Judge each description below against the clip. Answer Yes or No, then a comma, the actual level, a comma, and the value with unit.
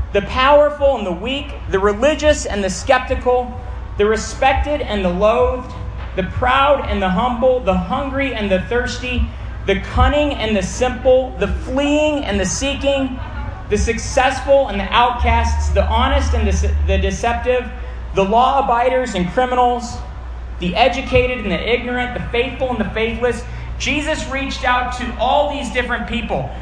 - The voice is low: No, high, 245 Hz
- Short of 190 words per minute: Yes, average, 155 wpm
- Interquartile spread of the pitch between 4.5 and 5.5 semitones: Yes, average, 4.9 semitones